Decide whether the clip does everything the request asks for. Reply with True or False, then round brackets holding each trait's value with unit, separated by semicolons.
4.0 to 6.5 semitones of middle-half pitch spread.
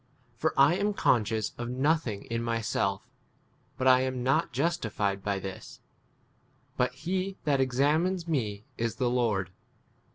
True (5.3 semitones)